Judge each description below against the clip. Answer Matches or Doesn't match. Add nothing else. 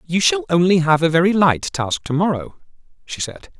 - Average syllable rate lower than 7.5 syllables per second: Matches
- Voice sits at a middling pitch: Matches